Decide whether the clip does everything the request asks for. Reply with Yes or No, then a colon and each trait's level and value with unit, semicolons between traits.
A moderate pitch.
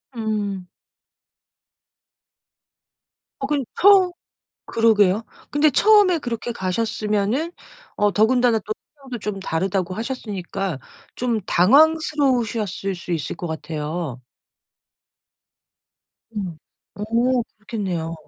No: high, 215 Hz